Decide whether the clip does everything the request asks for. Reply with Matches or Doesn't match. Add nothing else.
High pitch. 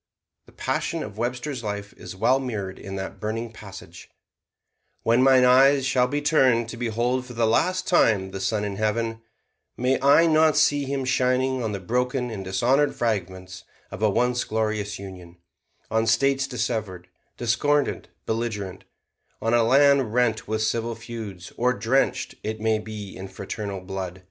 Doesn't match